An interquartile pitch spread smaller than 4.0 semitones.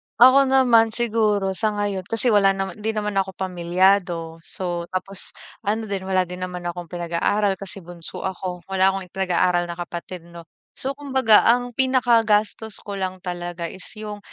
Yes: average, 3.4 semitones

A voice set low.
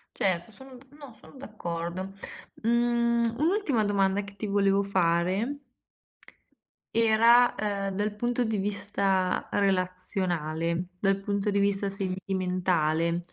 No: high, 200 Hz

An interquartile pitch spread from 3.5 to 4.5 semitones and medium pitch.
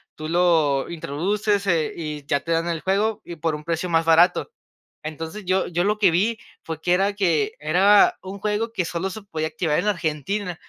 Yes: average, 3.9 semitones; medium, 175 Hz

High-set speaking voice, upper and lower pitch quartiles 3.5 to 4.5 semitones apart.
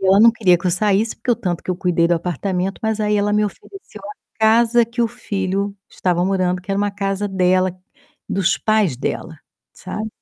No: high, 195 Hz; average, 2.9 semitones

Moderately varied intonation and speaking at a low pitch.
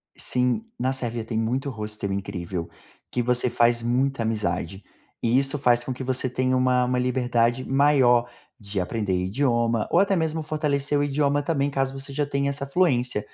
Yes: average, 3.1 semitones; low, 125 Hz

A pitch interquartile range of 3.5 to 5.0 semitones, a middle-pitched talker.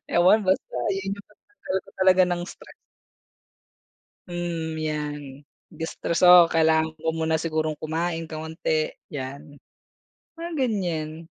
No: average, 2.8 semitones; medium, 165 Hz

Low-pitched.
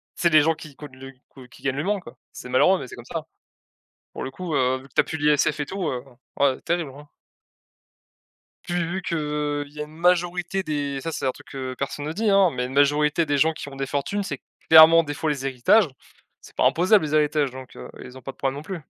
No: medium, 150 Hz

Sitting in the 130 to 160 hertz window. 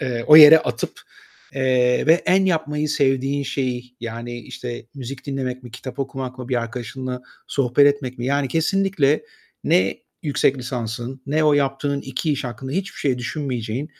Yes: low, 135 Hz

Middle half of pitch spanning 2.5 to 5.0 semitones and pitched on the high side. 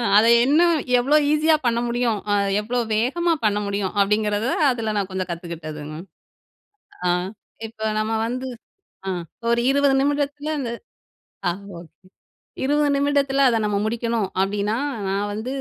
No: wide, 5.4 semitones; high, 230 Hz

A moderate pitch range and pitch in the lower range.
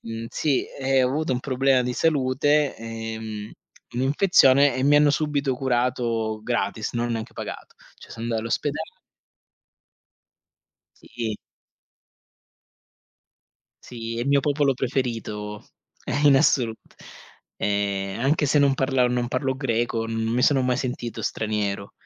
Yes: average, 3.2 semitones; low, 125 Hz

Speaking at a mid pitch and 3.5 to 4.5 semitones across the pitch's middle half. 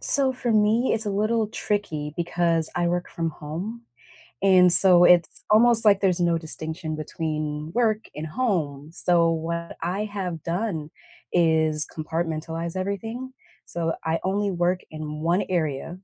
Yes: medium, 175 Hz; average, 4.2 semitones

